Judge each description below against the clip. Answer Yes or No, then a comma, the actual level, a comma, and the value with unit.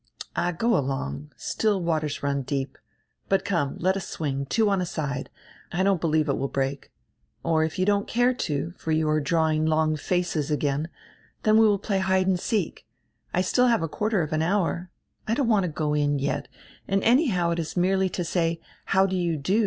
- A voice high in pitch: No, medium, 170 Hz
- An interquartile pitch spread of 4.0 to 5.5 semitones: Yes, average, 4.3 semitones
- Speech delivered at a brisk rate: Yes, fast, 210 wpm